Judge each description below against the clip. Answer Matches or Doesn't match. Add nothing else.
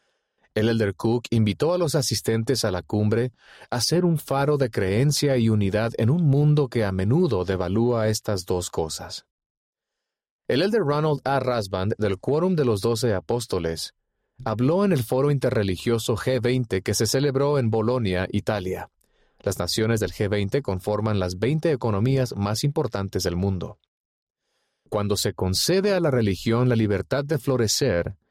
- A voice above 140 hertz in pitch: Doesn't match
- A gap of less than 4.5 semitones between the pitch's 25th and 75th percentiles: Doesn't match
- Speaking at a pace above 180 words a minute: Doesn't match